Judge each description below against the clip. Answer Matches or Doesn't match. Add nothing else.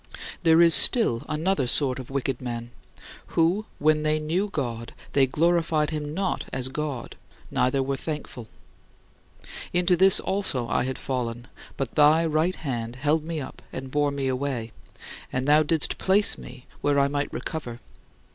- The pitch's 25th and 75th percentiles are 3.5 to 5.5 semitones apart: Matches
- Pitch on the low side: Doesn't match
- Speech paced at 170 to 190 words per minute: Doesn't match